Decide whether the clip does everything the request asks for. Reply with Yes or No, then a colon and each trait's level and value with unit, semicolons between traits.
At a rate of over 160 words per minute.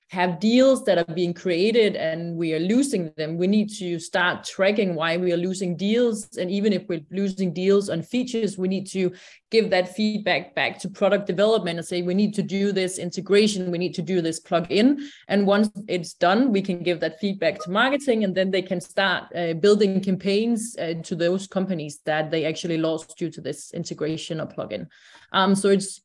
Yes: fast, 205 wpm